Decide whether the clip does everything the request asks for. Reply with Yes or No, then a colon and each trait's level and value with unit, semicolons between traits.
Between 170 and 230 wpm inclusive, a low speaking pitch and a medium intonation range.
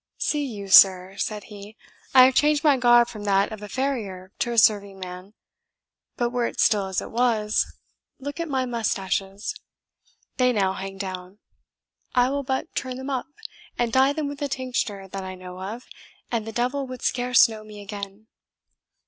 No: average, 180 wpm; high, 220 Hz; average, 4.6 semitones